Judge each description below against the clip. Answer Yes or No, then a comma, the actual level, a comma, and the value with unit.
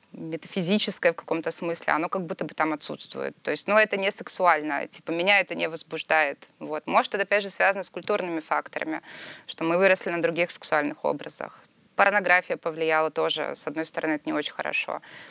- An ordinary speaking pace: No, fast, 185 wpm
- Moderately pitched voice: Yes, medium, 170 Hz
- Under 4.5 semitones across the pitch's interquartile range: Yes, average, 3.4 semitones